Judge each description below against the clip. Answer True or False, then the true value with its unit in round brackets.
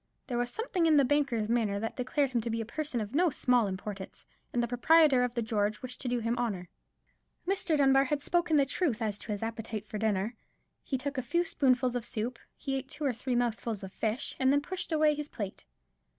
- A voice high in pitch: True (245 Hz)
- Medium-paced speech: False (235 wpm)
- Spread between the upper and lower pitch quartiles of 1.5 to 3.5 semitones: False (4.2 semitones)